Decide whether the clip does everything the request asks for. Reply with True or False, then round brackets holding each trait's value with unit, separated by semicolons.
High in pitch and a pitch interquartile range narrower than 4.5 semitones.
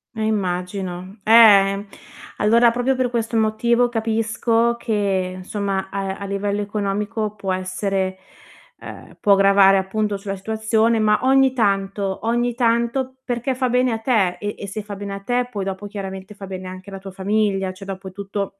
True (205 Hz; 2.7 semitones)